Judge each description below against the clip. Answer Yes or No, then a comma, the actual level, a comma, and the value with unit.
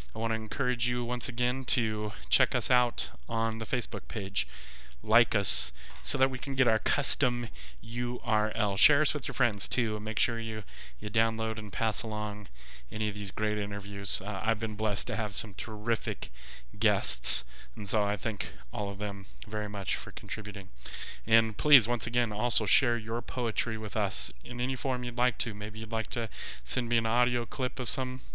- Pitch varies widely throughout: No, average, 2.8 semitones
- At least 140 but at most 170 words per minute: No, average, 195 wpm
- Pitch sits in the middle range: No, low, 110 Hz